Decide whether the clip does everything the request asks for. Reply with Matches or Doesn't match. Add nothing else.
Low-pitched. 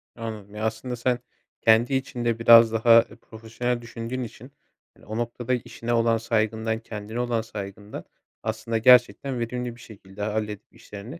Matches